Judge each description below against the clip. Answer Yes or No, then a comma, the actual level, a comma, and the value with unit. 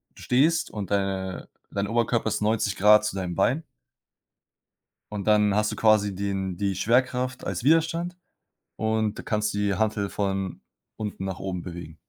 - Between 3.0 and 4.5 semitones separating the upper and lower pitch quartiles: No, narrow, 2.4 semitones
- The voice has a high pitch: No, low, 105 Hz